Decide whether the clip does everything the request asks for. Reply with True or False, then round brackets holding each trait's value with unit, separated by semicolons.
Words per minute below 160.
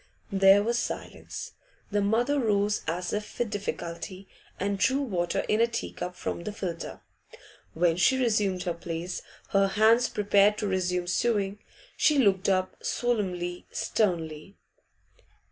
True (140 wpm)